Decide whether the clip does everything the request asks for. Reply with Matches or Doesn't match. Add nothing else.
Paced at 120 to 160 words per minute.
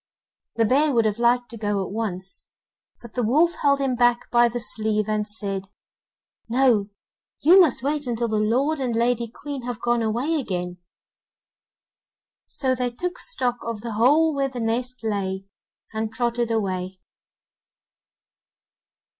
Matches